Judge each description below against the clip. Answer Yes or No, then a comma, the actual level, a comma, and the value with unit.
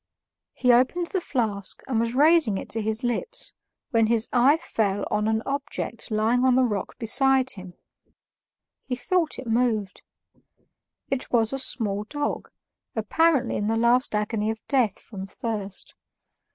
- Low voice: No, high, 235 Hz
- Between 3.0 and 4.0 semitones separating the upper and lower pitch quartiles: Yes, average, 3.7 semitones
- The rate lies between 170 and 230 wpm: No, average, 150 wpm